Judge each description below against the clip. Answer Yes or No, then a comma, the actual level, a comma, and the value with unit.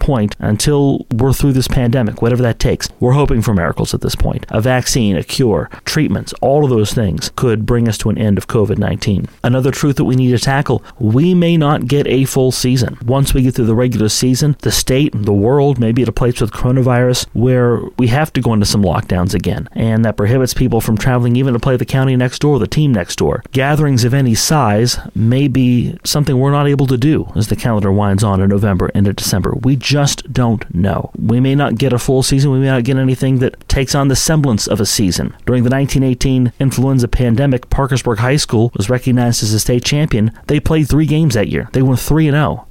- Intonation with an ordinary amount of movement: Yes, average, 3.5 semitones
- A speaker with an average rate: No, fast, 230 wpm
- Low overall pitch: Yes, low, 125 Hz